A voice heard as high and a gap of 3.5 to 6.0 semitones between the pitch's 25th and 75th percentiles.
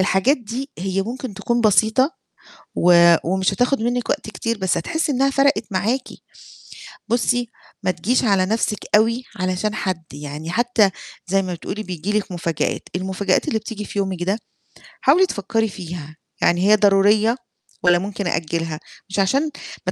Yes: high, 200 Hz; average, 4.1 semitones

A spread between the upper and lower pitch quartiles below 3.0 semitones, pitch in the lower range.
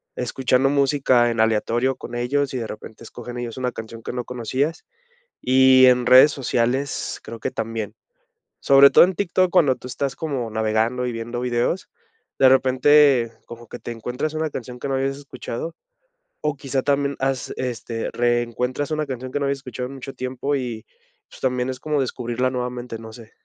Yes: narrow, 2.4 semitones; low, 125 Hz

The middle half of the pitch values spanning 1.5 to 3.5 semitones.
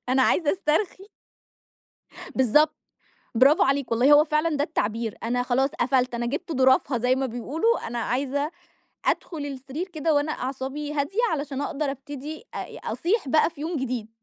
Yes: average, 3.1 semitones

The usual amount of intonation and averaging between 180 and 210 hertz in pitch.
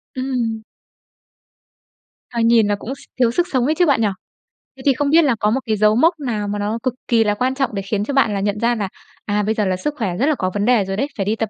No: average, 4.1 semitones; high, 225 Hz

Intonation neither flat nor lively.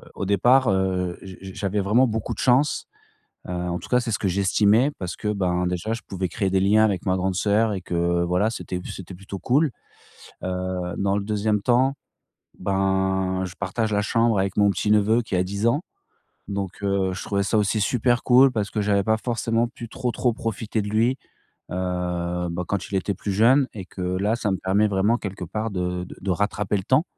Yes: average, 3.1 semitones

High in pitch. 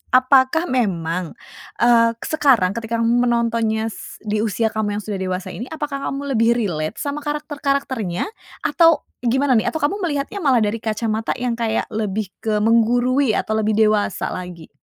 Yes: high, 230 Hz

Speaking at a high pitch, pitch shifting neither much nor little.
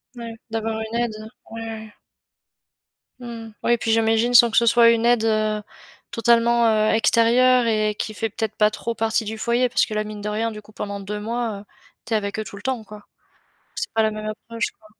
No: high, 225 Hz; narrow, 1.5 semitones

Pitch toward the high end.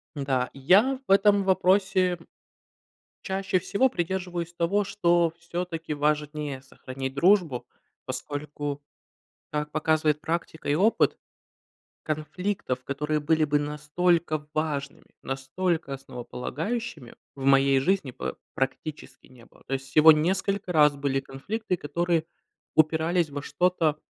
No: medium, 155 Hz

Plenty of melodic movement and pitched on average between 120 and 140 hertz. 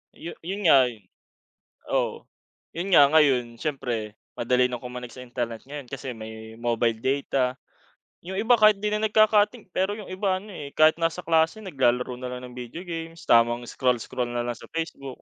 Yes: wide, 6.5 semitones; low, 135 Hz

